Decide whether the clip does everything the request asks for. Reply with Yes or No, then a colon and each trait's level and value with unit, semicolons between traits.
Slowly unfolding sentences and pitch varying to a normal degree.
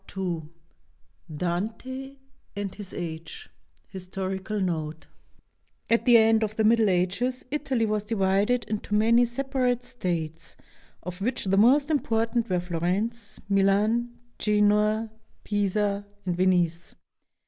Yes: slow, 115 wpm; average, 4.0 semitones